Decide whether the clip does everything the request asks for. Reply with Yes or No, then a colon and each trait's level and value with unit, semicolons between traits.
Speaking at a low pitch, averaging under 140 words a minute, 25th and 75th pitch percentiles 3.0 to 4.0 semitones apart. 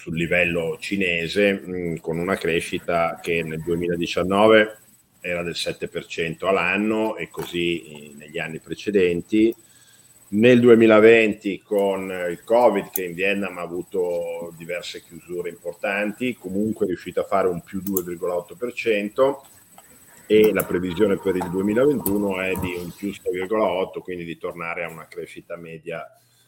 Yes: very low, 95 Hz; average, 130 wpm; average, 3.7 semitones